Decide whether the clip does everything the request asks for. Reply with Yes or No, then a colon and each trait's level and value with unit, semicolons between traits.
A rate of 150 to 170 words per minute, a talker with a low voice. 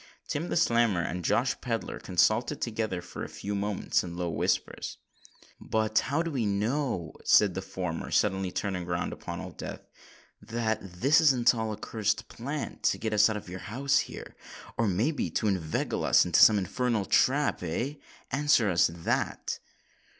Yes: average, 165 wpm; low, 105 Hz